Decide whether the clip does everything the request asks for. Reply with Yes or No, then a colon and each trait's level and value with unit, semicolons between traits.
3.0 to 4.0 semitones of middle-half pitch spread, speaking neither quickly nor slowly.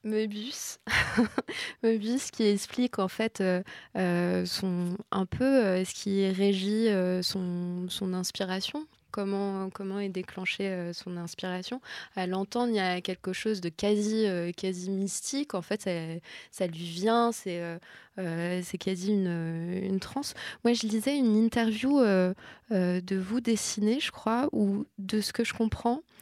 Yes: average, 3.5 semitones; average, 160 wpm